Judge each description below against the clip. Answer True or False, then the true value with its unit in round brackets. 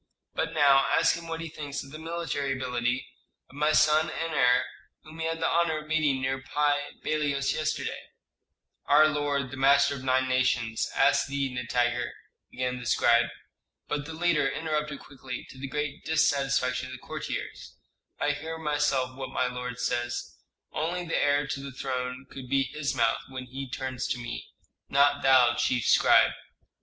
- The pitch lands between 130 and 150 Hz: True (140 Hz)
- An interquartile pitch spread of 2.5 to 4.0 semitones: True (3.0 semitones)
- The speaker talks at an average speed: True (175 wpm)